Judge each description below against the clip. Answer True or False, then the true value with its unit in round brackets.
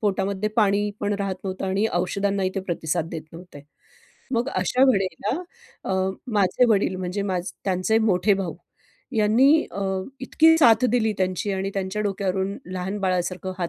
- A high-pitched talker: True (195 Hz)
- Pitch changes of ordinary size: False (2.0 semitones)